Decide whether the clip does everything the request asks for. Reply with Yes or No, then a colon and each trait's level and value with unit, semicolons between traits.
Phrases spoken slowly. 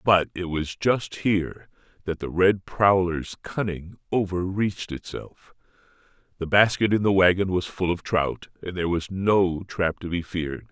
No: average, 160 wpm